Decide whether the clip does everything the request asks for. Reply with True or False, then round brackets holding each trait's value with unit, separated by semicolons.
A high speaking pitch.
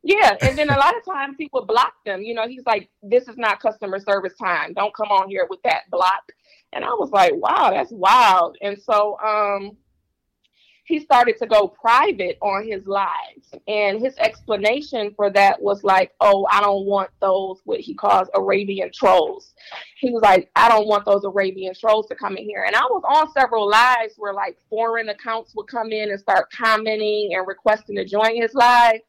True (215 Hz)